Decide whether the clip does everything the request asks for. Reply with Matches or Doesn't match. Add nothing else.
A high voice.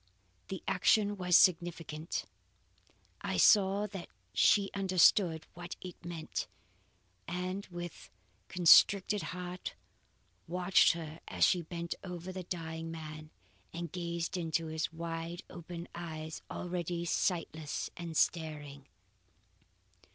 Doesn't match